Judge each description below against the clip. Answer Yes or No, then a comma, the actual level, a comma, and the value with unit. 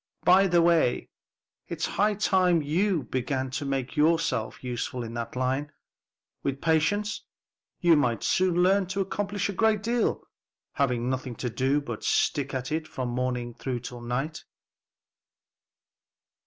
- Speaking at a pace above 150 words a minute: No, average, 140 wpm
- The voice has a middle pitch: Yes, medium, 145 Hz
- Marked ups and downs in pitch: Yes, wide, 6.2 semitones